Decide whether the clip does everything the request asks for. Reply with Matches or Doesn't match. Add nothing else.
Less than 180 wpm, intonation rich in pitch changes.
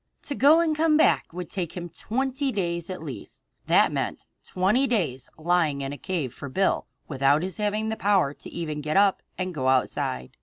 Doesn't match